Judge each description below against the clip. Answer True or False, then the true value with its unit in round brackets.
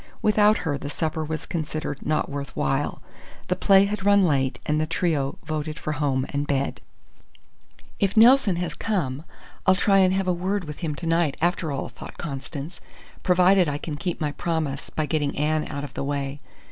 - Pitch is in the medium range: True (155 Hz)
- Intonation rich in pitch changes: False (4.2 semitones)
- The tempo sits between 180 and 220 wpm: True (190 wpm)